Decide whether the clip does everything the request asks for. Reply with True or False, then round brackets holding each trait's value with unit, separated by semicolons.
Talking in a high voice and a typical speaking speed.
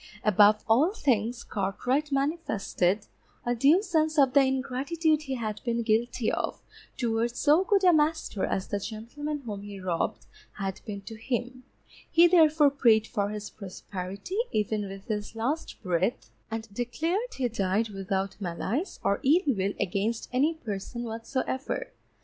True (235 Hz; 150 wpm)